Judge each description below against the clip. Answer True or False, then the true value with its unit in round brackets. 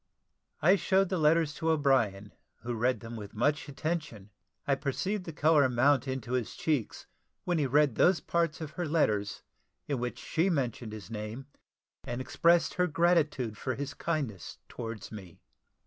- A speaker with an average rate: True (165 wpm)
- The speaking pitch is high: False (140 Hz)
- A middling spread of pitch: False (5.7 semitones)